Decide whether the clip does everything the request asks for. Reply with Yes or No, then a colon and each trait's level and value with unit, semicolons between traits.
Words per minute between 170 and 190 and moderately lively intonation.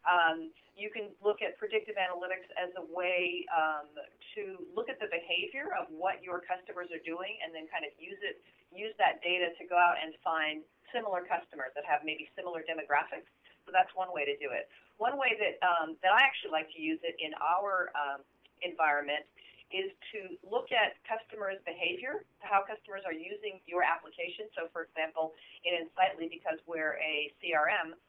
Yes: average, 185 wpm; average, 4.6 semitones